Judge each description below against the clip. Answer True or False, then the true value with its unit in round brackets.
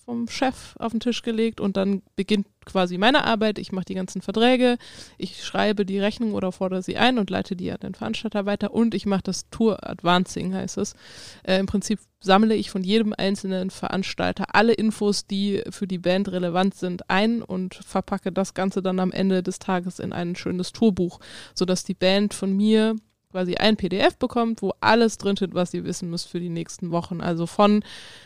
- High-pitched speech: True (195 Hz)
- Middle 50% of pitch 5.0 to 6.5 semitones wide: False (2.7 semitones)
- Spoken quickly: True (200 wpm)